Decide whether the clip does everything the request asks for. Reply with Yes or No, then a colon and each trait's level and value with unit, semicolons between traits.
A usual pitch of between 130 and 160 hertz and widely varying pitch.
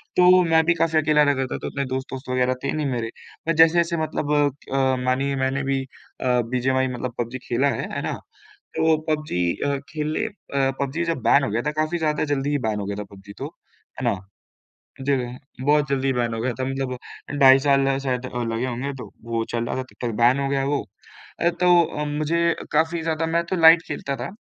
No: medium, 140 Hz; average, 3.6 semitones